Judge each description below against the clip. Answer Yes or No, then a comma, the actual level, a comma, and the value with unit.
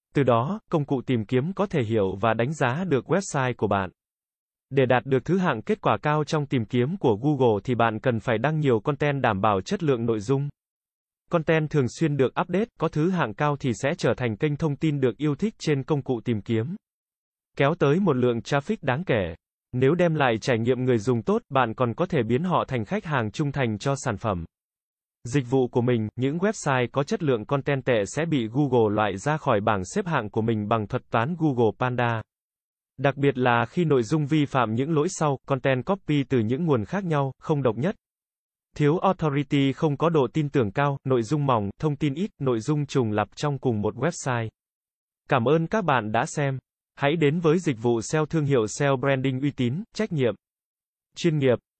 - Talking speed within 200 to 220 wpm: Yes, average, 215 wpm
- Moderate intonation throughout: Yes, average, 4.0 semitones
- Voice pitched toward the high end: No, medium, 140 Hz